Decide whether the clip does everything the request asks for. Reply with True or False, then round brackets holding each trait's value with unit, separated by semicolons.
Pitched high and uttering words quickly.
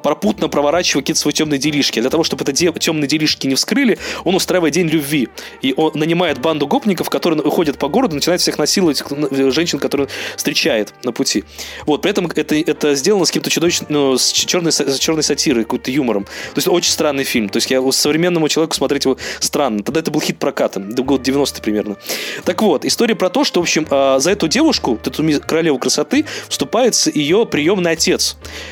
False (155 Hz; 200 wpm)